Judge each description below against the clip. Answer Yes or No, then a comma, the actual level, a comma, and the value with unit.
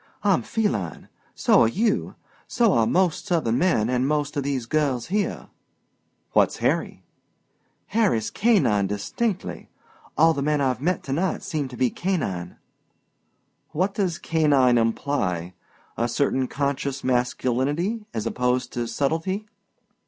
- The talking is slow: Yes, slow, 130 wpm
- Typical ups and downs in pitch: No, wide, 6.4 semitones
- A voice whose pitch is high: No, medium, 140 Hz